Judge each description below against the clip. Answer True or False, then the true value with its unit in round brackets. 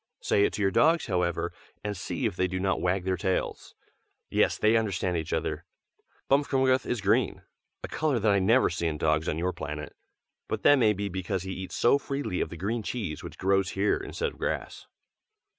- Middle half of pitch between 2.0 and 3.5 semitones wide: False (4.3 semitones)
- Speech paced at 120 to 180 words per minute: False (205 wpm)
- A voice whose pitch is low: True (100 Hz)